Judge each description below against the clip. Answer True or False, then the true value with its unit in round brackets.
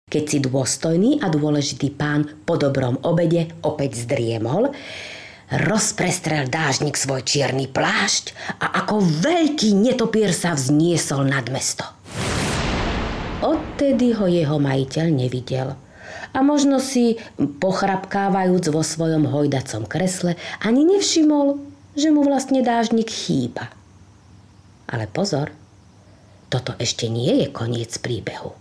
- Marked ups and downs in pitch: True (7.4 semitones)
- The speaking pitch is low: False (155 Hz)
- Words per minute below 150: True (110 wpm)